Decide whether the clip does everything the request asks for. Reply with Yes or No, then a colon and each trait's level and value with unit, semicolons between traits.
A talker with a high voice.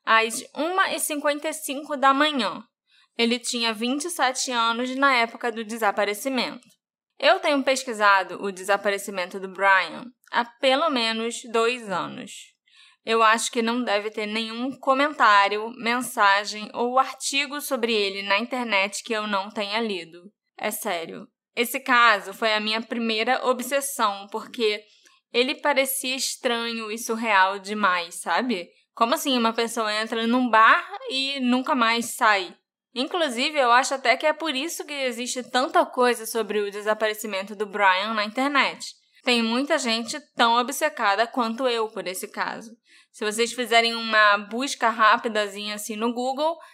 Yes: high, 235 Hz